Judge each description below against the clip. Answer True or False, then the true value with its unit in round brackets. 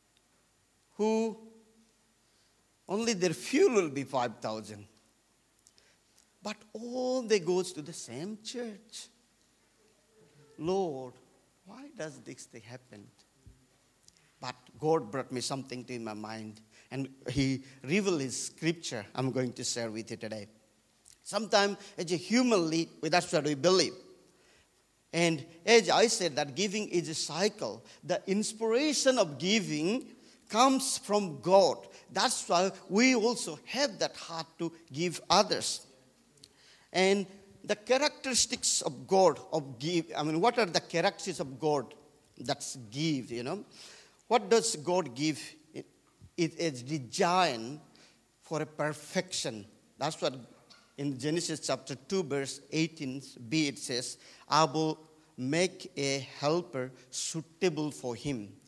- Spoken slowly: True (125 wpm)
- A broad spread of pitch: True (7.2 semitones)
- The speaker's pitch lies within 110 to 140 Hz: False (160 Hz)